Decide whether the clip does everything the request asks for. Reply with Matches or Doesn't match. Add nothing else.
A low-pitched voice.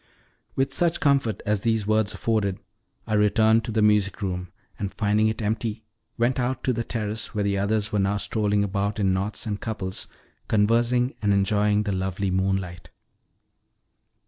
Matches